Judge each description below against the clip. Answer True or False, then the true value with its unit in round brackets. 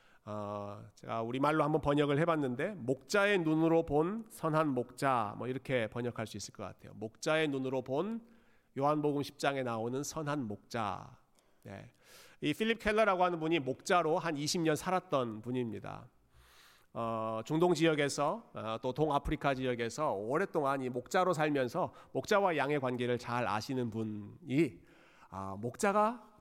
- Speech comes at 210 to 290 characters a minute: False (300 characters per minute)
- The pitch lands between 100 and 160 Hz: True (140 Hz)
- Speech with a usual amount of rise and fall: True (5.0 semitones)